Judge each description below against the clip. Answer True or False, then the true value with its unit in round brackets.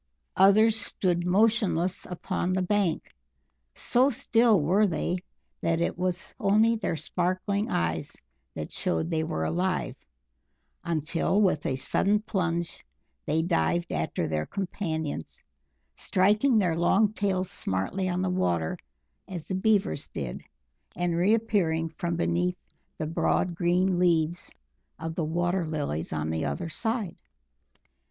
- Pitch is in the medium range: True (175 Hz)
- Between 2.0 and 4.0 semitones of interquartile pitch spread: True (3.5 semitones)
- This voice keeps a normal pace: False (130 wpm)